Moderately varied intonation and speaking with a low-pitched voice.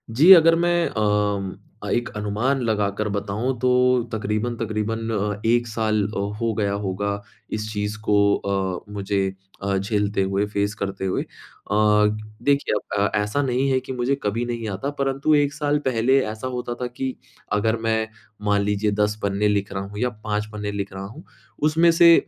Yes: average, 3.4 semitones; low, 105 Hz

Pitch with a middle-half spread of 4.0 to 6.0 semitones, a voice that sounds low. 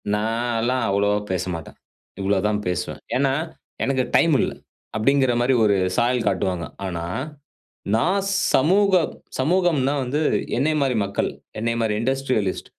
Yes: average, 5.0 semitones; low, 120 Hz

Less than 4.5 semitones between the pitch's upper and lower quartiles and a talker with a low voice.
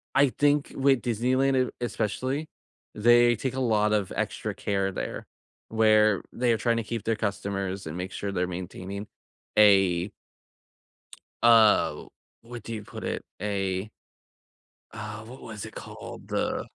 Yes: average, 3.3 semitones; low, 110 Hz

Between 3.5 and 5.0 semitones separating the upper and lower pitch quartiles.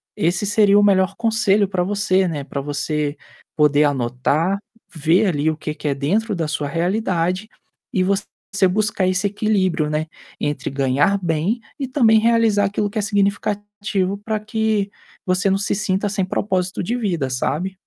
Yes: average, 4.7 semitones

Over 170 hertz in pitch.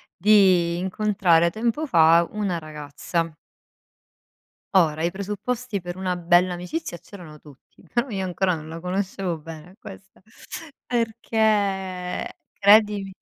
Yes: medium, 185 Hz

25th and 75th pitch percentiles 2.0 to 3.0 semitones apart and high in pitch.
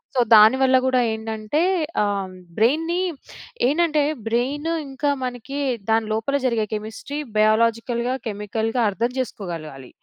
No: average, 3.7 semitones; high, 230 Hz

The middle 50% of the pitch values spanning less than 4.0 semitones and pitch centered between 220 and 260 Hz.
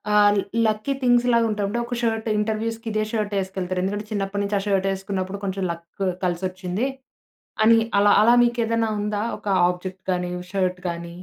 No: average, 2.9 semitones; high, 205 Hz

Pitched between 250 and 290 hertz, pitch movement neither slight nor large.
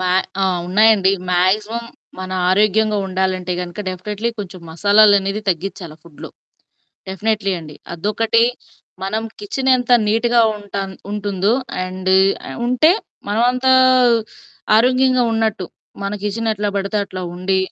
No: high, 205 Hz; average, 3.0 semitones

